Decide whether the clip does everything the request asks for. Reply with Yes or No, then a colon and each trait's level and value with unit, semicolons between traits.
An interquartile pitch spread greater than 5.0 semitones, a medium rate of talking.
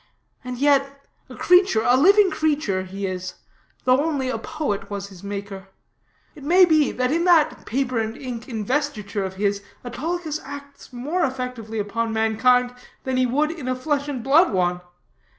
Yes: wide, 5.4 semitones; average, 170 wpm